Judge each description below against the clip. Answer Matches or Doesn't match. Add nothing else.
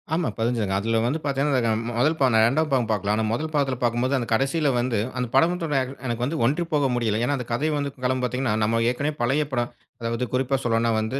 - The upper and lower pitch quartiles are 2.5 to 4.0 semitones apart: Matches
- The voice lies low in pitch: Matches